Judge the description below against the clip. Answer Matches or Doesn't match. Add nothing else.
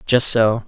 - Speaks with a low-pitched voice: Matches